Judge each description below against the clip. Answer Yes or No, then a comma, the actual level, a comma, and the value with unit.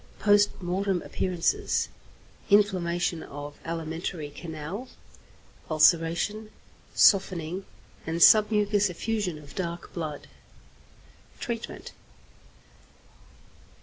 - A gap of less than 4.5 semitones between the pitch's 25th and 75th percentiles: Yes, average, 4.0 semitones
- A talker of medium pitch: Yes, medium, 180 Hz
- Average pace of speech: No, slow, 70 wpm